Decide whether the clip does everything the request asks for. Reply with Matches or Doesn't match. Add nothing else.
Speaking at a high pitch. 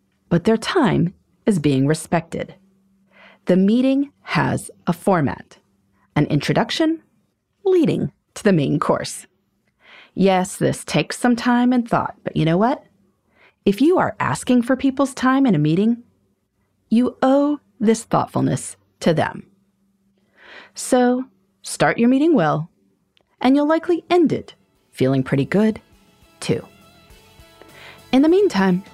Matches